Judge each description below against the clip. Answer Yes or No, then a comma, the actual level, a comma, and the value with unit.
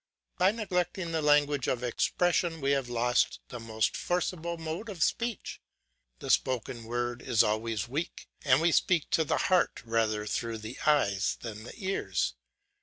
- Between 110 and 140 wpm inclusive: No, average, 160 wpm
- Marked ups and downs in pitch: Yes, wide, 6.8 semitones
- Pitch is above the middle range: No, low, 135 Hz